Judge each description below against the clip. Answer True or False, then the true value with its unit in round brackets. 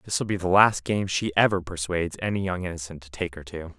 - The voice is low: True (90 Hz)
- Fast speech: True (255 wpm)